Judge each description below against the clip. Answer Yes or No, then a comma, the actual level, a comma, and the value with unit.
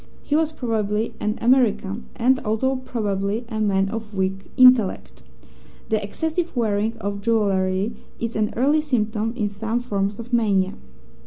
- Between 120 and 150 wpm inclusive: Yes, average, 145 wpm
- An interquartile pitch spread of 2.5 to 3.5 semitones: Yes, average, 3.2 semitones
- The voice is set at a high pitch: Yes, high, 220 Hz